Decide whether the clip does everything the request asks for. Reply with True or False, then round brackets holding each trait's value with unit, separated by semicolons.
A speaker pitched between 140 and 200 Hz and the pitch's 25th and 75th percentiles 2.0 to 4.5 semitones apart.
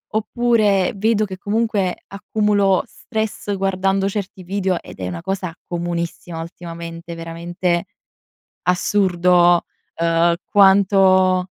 True (185 Hz; 2.6 semitones)